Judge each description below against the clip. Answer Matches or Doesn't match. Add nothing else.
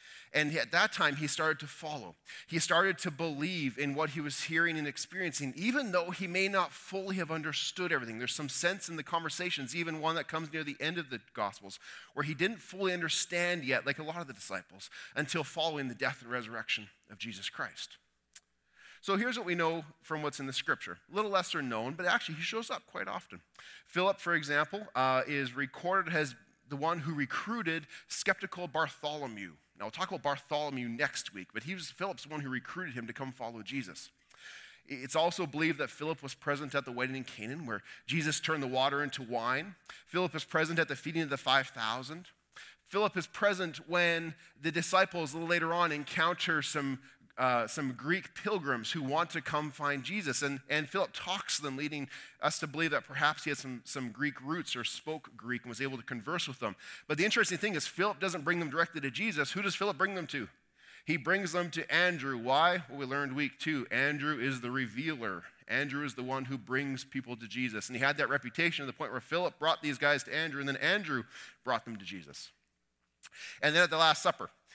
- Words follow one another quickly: Matches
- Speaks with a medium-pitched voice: Matches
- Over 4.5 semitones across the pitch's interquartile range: Doesn't match